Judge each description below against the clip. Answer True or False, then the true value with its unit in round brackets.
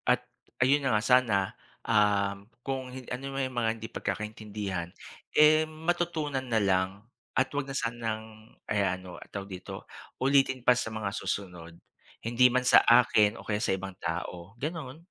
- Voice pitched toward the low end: True (115 Hz)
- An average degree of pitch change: True (4.8 semitones)